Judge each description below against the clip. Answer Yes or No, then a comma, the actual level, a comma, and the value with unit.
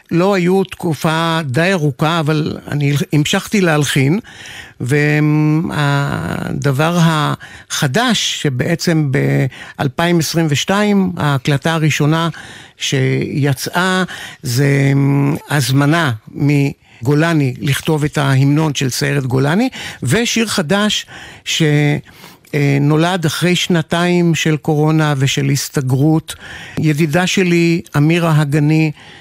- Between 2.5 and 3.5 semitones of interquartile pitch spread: Yes, average, 2.9 semitones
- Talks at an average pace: No, slow, 80 wpm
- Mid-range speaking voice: Yes, medium, 155 Hz